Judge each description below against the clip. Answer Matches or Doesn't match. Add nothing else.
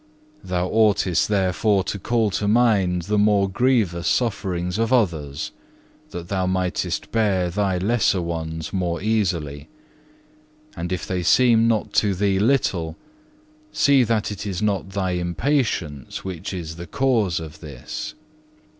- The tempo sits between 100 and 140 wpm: Matches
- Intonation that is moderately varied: Matches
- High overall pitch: Doesn't match